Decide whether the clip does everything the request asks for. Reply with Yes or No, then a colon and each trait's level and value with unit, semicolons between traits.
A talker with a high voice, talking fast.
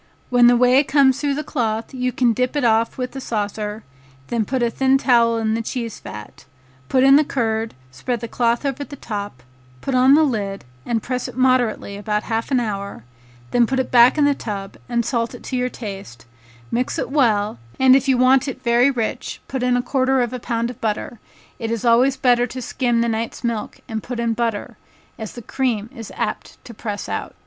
Yes: high, 240 Hz; fast, 215 wpm